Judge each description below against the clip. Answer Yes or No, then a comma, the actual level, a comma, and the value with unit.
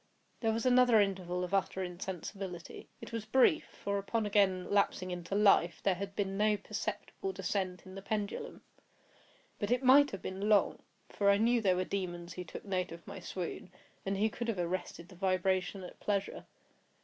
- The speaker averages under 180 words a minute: No, average, 185 wpm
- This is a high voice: Yes, high, 195 Hz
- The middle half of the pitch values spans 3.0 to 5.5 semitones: No, narrow, 2.4 semitones